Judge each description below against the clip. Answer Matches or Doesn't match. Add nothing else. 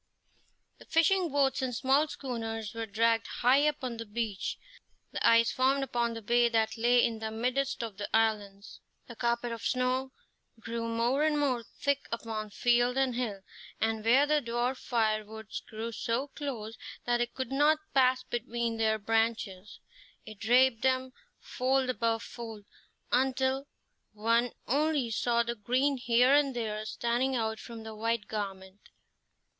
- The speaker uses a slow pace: Doesn't match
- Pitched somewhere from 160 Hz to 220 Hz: Doesn't match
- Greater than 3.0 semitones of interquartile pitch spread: Doesn't match